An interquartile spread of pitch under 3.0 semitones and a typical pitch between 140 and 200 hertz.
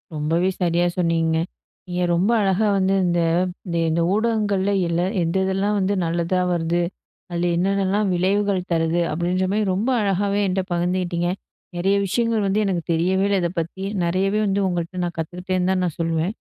Yes: narrow, 2.4 semitones; medium, 185 Hz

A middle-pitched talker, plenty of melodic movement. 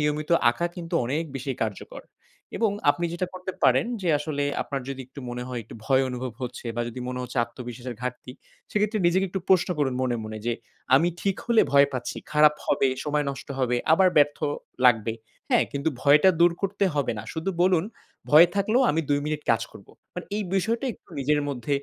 Yes: medium, 145 Hz; wide, 5.7 semitones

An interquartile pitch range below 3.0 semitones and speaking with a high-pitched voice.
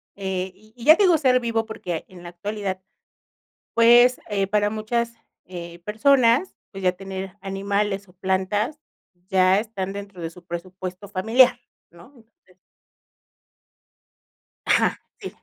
No: average, 3.7 semitones; high, 200 Hz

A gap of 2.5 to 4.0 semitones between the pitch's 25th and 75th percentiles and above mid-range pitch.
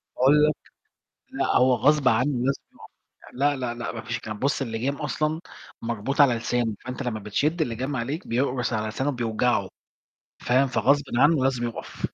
No: average, 3.3 semitones; low, 125 Hz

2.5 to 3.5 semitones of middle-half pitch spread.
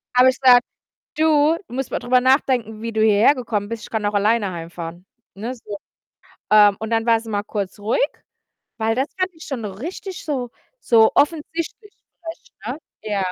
No: average, 4.3 semitones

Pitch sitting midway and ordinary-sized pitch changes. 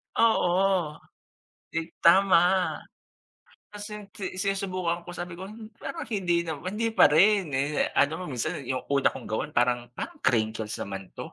No: medium, 175 Hz; wide, 5.8 semitones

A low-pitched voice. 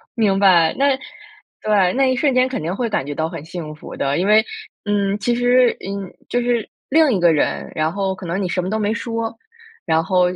No: high, 200 Hz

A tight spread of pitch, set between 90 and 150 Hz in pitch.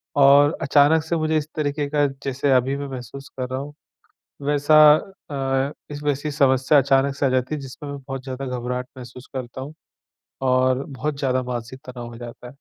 Yes: narrow, 2.1 semitones; low, 135 Hz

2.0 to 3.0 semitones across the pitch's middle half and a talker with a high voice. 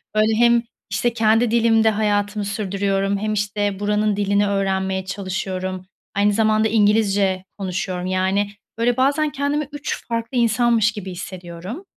Yes: narrow, 2.6 semitones; high, 205 Hz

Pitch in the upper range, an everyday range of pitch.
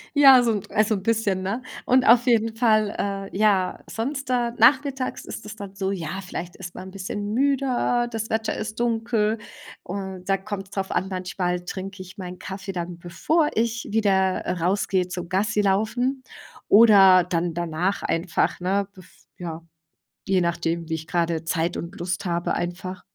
Yes: high, 195 Hz; average, 3.8 semitones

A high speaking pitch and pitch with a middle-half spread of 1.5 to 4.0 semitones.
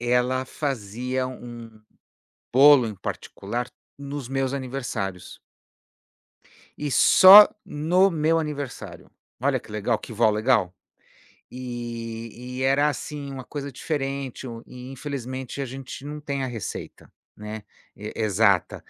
No: low, 130 Hz; average, 3.4 semitones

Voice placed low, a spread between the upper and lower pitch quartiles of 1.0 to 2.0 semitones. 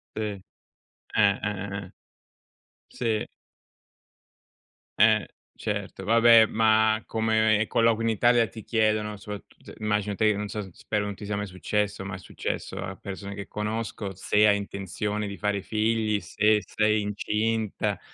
Yes: low, 105 Hz; narrow, 1.5 semitones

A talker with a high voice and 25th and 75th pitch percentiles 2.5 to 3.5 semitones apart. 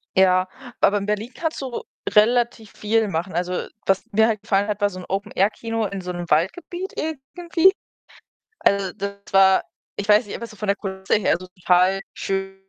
Yes: high, 200 Hz; average, 2.9 semitones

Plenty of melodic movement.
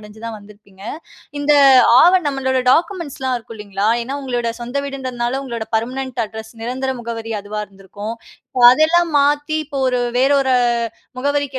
No: average, 3.8 semitones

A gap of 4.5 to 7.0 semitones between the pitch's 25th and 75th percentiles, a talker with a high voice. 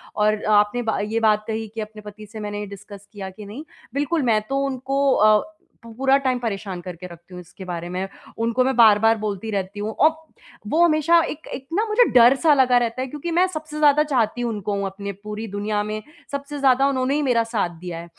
Yes: average, 4.8 semitones; high, 225 Hz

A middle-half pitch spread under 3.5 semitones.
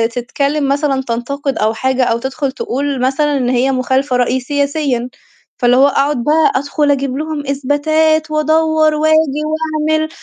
Yes: average, 2.8 semitones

